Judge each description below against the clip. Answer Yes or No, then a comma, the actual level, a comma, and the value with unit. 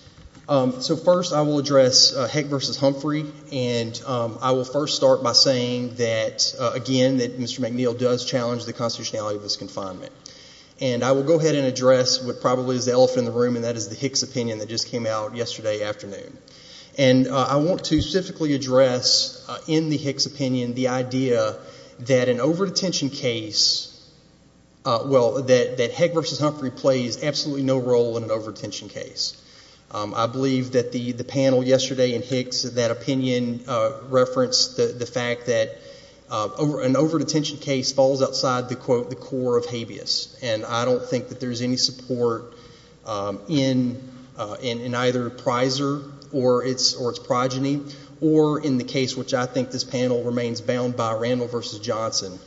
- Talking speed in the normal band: Yes, average, 180 wpm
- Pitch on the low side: Yes, low, 130 Hz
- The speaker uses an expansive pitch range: No, narrow, 2.4 semitones